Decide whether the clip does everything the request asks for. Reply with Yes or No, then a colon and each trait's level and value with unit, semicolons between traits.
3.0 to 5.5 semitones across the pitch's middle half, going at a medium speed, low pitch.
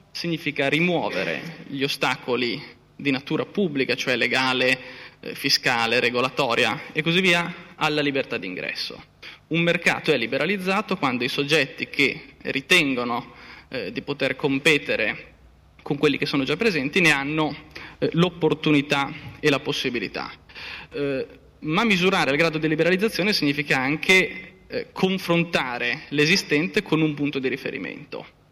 No: average, 3.9 semitones; average, 125 wpm; medium, 150 Hz